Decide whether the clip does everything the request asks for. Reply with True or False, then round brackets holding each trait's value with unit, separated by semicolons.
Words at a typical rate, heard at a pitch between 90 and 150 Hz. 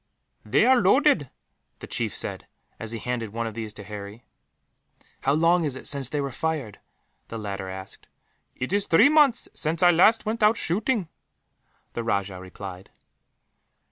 True (165 wpm; 135 Hz)